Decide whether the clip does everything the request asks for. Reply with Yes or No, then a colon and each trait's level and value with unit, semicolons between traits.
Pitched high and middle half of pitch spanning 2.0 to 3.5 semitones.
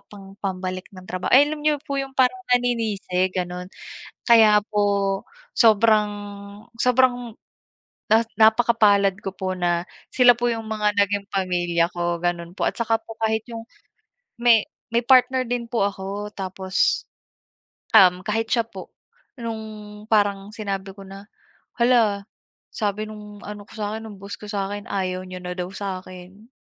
Yes: high, 205 Hz; average, 3.0 semitones